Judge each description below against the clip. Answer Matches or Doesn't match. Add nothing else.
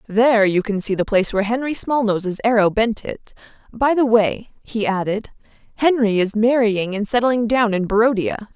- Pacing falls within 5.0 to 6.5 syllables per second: Matches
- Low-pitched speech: Doesn't match